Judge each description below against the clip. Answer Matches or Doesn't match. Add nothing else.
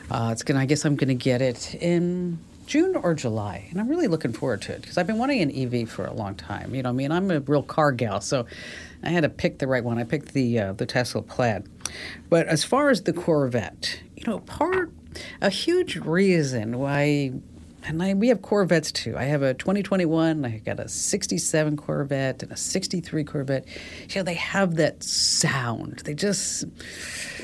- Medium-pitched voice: Matches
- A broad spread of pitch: Matches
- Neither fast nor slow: Doesn't match